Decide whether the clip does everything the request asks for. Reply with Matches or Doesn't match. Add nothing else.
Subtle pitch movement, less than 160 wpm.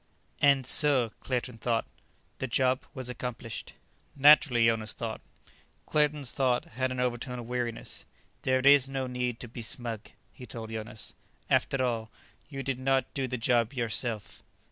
Matches